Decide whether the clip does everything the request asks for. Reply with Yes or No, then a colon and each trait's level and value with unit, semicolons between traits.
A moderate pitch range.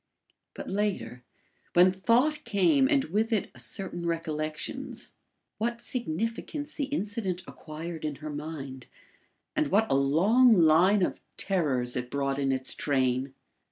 No: wide, 8.0 semitones